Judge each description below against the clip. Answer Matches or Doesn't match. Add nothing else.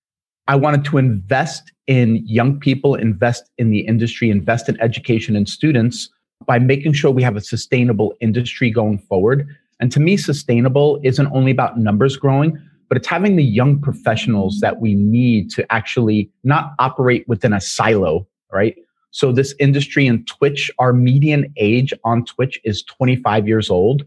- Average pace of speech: Matches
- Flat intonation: Doesn't match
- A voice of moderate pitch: Doesn't match